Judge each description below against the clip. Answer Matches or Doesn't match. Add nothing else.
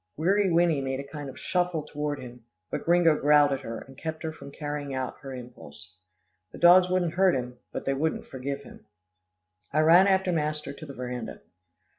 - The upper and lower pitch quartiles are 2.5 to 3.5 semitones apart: Doesn't match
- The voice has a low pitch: Doesn't match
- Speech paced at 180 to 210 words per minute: Matches